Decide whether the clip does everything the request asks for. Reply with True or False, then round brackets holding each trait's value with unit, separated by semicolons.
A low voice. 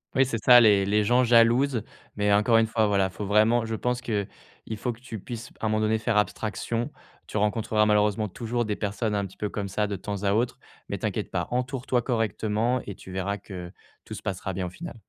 True (110 Hz)